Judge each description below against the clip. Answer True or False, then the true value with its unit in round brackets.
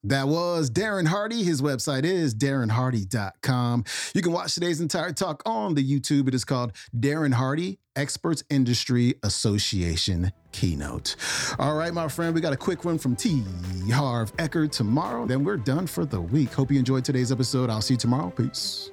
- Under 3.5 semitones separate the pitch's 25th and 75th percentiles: False (4.9 semitones)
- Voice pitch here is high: False (140 Hz)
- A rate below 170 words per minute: False (180 wpm)